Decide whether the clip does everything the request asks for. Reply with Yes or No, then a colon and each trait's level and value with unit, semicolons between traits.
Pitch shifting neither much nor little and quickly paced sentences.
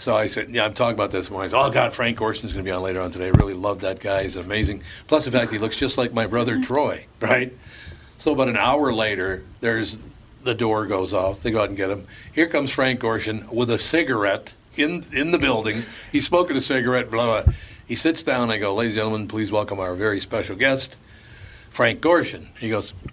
Yes: average, 3.7 semitones; fast, 235 wpm